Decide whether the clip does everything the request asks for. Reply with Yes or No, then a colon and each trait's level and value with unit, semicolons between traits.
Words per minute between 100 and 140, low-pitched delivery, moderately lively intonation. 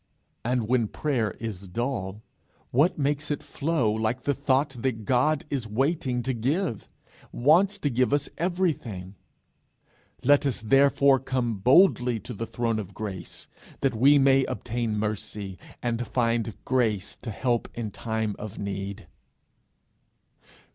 Yes: slow, 135 wpm; low, 120 Hz; average, 4.1 semitones